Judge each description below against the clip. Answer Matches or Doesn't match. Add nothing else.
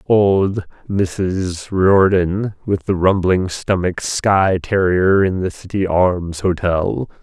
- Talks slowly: Matches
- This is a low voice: Matches